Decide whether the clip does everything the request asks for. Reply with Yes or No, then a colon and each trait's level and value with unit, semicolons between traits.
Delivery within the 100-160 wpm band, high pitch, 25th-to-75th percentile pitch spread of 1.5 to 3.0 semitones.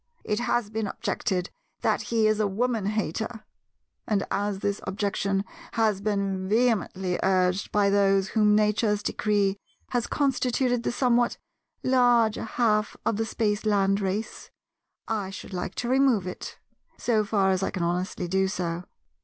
Yes: average, 145 wpm; high, 210 Hz; average, 2.7 semitones